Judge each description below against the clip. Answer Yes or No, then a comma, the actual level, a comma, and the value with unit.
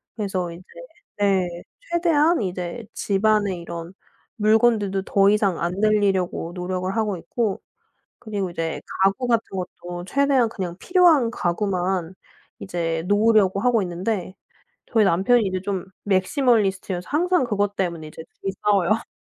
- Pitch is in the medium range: No, high, 195 Hz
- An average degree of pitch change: Yes, average, 3.5 semitones